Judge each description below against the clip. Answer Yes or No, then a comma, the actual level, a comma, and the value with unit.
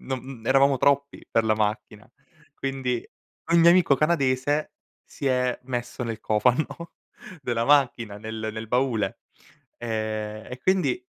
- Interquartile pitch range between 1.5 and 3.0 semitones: No, average, 3.9 semitones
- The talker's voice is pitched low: Yes, low, 125 Hz